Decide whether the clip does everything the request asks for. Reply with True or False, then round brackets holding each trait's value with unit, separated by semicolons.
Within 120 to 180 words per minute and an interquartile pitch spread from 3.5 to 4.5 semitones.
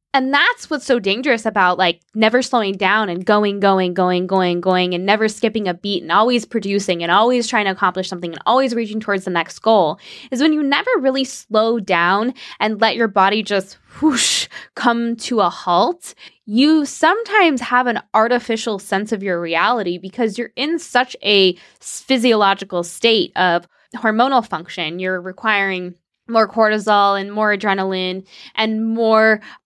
True (165 wpm; 4.2 semitones)